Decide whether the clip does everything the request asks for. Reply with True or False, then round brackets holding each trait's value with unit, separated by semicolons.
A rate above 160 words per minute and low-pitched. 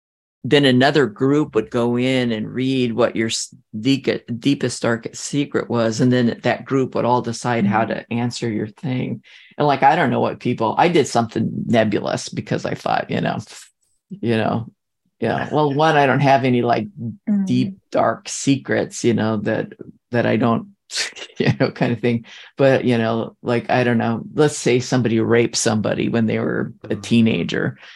True (180 wpm; 120 Hz)